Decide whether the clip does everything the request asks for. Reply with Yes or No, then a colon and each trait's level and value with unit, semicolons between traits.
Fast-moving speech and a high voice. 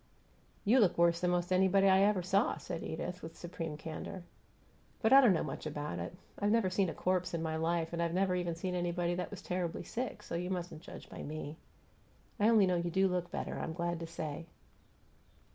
No: fast, 215 wpm; medium, 175 Hz